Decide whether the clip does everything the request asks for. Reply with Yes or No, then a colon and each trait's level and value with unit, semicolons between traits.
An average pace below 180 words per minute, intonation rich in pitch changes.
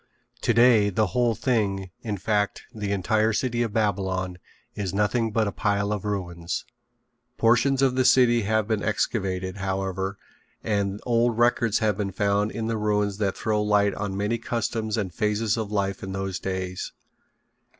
No: average, 160 wpm; narrow, 2.4 semitones